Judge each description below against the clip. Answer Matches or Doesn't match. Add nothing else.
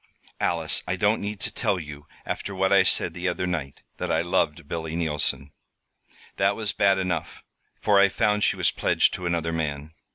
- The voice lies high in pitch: Doesn't match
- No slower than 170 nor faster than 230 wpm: Matches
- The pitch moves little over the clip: Doesn't match